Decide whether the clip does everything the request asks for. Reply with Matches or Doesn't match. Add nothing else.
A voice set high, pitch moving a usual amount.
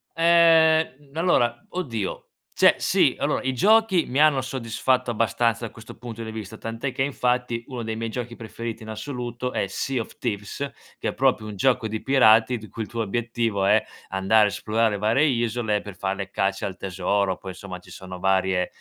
Doesn't match